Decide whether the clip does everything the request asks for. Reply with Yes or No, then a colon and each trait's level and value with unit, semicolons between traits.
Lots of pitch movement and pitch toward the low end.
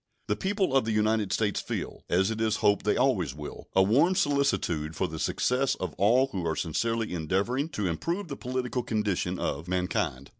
Yes: wide, 6.1 semitones; low, 105 Hz